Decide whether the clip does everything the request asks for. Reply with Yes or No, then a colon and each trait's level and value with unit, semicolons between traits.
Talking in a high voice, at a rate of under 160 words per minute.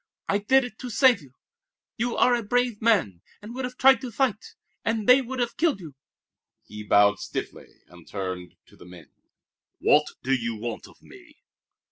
No: high, 215 Hz; average, 185 wpm